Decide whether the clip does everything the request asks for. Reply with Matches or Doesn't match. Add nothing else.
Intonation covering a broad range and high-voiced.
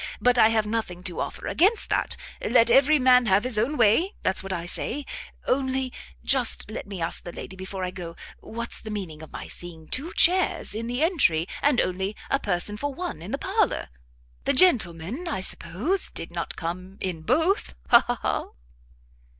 Matches